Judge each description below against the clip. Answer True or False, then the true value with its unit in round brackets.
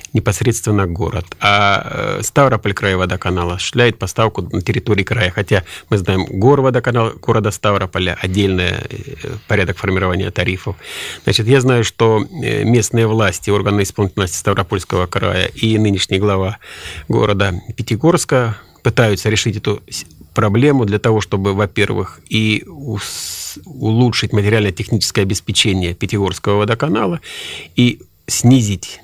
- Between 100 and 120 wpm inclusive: True (110 wpm)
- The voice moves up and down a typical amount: True (3.0 semitones)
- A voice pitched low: True (105 Hz)